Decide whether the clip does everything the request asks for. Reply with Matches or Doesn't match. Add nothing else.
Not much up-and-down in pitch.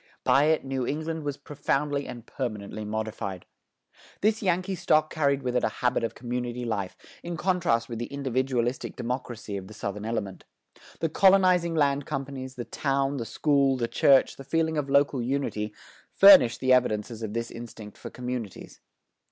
Doesn't match